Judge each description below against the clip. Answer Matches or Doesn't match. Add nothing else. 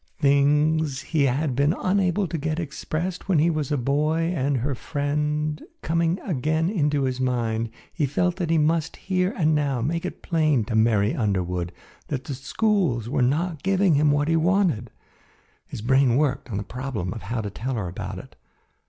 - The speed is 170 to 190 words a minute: Matches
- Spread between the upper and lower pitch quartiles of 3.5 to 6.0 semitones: Matches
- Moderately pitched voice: Matches